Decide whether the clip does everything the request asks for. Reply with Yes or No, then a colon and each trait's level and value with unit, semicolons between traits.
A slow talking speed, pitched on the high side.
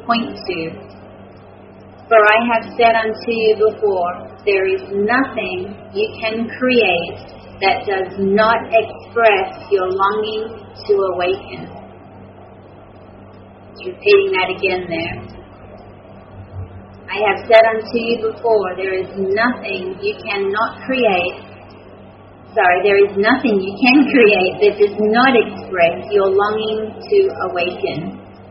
Yes: slow, 115 wpm; high, 200 Hz